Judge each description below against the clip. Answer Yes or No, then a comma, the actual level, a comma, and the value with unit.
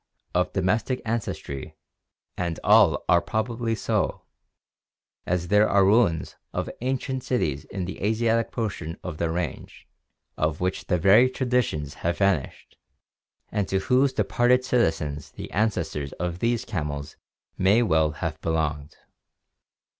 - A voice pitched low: Yes, very low, 95 Hz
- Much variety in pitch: Yes, wide, 6.2 semitones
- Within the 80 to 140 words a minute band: Yes, slow, 135 wpm